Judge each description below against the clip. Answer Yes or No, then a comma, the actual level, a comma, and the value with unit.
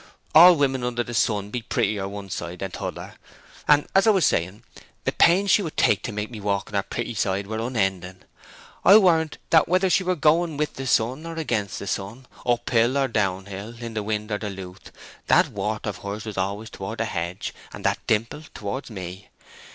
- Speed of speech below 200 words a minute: No, fast, 205 wpm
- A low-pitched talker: Yes, low, 110 Hz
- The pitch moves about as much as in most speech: No, wide, 6.0 semitones